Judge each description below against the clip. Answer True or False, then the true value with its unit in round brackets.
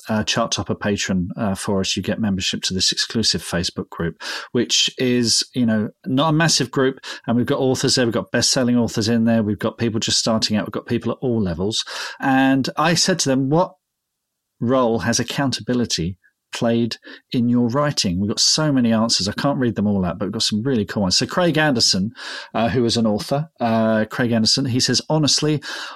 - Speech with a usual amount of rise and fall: True (3.5 semitones)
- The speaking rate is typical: False (215 wpm)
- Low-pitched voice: True (115 Hz)